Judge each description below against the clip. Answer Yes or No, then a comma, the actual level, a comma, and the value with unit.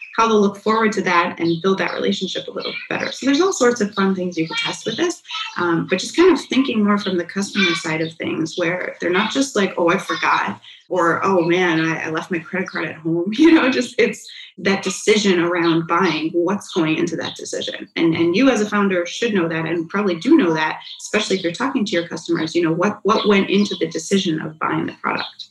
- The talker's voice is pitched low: No, high, 190 Hz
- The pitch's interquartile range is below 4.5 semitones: No, average, 4.9 semitones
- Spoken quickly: Yes, fast, 240 wpm